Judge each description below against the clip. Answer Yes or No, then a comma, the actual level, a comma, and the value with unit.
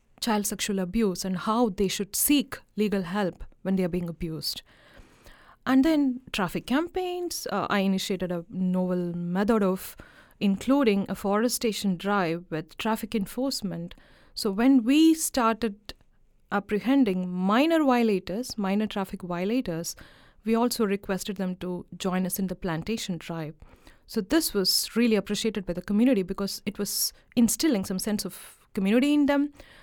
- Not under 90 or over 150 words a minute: Yes, average, 145 wpm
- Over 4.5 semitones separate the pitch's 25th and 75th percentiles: No, average, 4.1 semitones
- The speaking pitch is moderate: No, high, 205 Hz